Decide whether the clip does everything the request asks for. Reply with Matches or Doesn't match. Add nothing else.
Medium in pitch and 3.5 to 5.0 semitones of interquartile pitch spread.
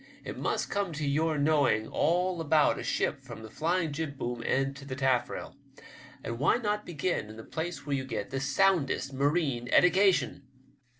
Matches